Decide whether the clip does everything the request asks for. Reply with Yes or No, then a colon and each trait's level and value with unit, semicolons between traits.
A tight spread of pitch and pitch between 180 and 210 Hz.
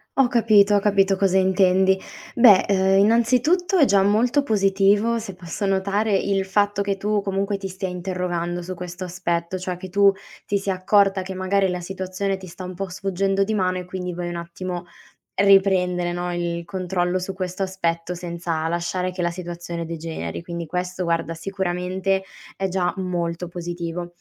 Yes: narrow, 2.0 semitones; medium, 185 Hz